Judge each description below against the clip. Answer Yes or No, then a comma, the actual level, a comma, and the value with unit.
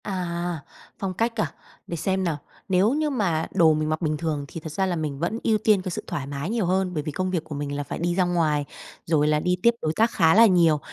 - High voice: No, medium, 170 Hz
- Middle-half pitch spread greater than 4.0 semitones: No, average, 3.7 semitones